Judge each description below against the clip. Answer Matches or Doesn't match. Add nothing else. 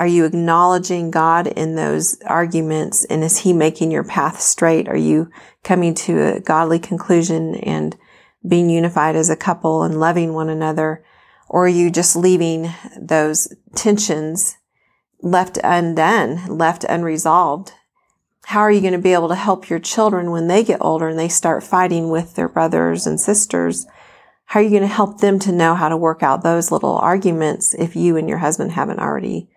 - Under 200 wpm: Matches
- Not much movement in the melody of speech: Matches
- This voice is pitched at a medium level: Matches